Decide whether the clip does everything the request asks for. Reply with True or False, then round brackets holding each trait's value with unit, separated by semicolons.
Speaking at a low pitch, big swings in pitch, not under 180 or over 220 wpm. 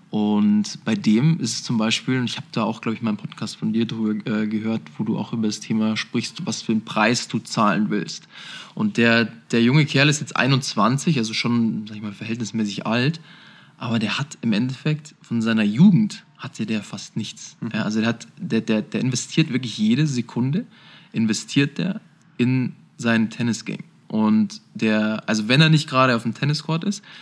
True (125 Hz; 6.3 semitones; 190 wpm)